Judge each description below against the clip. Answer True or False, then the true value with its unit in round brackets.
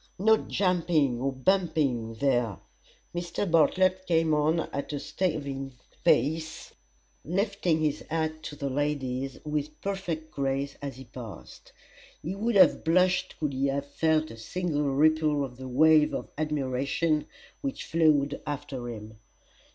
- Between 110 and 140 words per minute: True (135 wpm)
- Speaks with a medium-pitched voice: True (150 Hz)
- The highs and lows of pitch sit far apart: False (3.4 semitones)